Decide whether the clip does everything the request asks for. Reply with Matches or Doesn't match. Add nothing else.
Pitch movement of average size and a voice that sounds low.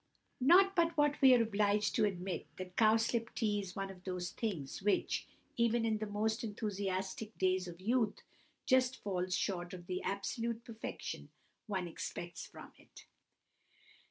Doesn't match